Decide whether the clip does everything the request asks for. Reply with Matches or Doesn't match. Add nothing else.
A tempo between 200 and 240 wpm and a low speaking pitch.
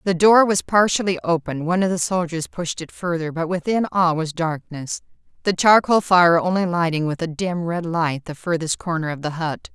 Doesn't match